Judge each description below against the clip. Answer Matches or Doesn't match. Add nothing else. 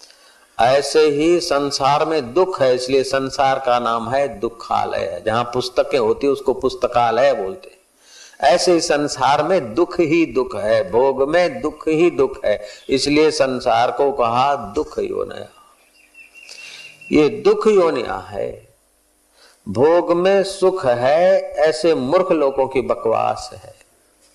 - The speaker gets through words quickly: Doesn't match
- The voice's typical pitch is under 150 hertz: Doesn't match